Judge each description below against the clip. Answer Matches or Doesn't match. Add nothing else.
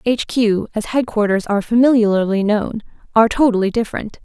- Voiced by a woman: Matches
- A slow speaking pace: Matches